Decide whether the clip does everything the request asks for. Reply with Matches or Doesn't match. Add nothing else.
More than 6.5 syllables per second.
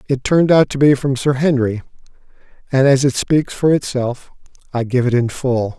Doesn't match